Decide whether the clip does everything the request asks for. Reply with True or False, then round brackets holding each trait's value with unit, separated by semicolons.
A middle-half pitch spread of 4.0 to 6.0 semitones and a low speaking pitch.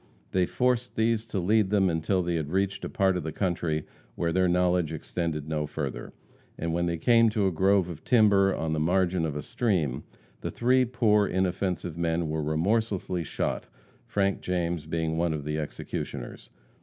False (3.6 semitones; 90 Hz)